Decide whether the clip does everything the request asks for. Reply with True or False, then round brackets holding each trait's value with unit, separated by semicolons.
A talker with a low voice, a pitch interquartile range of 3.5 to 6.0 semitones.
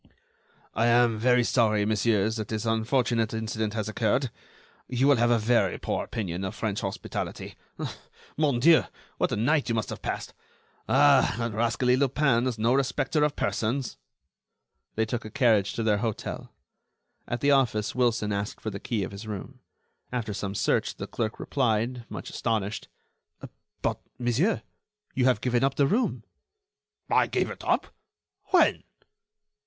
False (115 Hz; 2.8 semitones)